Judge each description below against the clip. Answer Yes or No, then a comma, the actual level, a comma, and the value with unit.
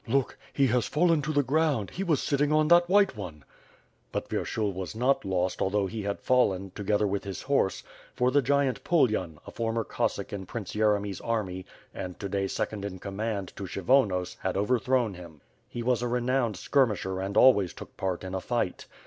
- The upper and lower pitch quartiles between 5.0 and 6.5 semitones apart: Yes, average, 5.3 semitones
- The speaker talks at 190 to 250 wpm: Yes, average, 195 wpm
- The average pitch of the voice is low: Yes, low, 110 Hz